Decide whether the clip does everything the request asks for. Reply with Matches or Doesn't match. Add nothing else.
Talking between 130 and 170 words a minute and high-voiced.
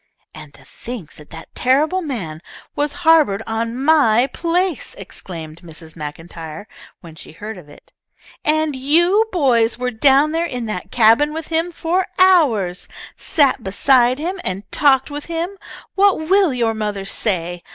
Matches